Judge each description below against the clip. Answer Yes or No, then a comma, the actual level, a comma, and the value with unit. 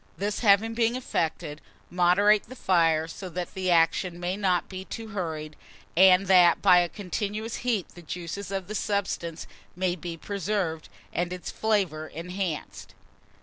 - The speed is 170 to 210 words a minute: No, average, 150 wpm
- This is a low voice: No, medium, 185 Hz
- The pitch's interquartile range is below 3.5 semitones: Yes, average, 3.0 semitones